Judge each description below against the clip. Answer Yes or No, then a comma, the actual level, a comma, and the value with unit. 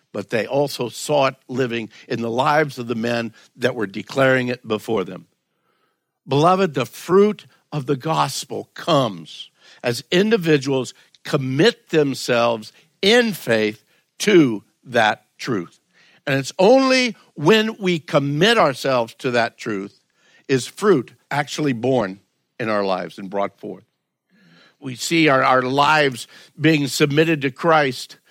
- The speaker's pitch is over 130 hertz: Yes, medium, 140 Hz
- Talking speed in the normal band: No, slow, 130 wpm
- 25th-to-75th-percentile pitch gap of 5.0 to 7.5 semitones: No, average, 4.5 semitones